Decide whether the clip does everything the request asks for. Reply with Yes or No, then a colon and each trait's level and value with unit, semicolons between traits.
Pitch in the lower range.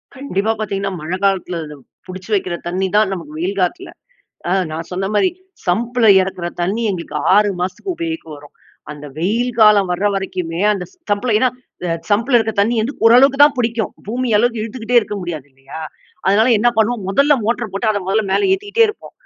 No: high, 205 Hz